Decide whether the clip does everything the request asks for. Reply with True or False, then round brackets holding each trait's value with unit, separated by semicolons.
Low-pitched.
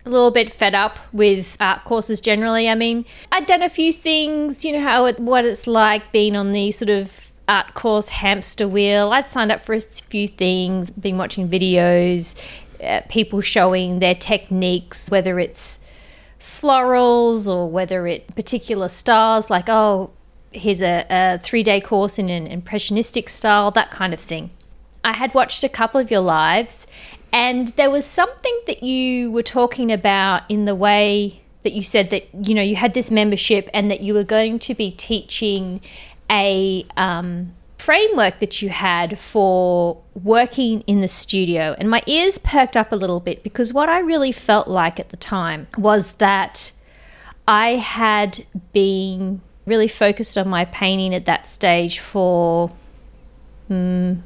False (205 Hz)